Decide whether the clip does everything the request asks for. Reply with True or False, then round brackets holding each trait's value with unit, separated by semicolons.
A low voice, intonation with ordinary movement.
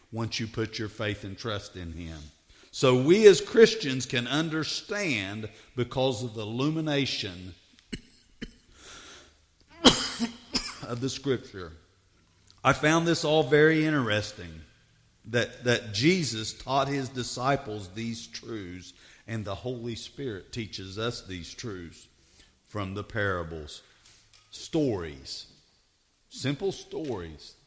False (115 Hz; 5.8 semitones)